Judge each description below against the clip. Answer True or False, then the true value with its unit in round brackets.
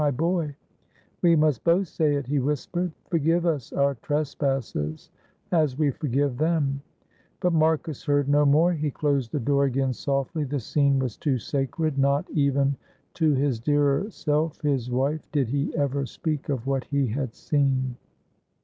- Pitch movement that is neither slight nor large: False (2.2 semitones)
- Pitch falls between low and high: True (145 Hz)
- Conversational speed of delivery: True (160 wpm)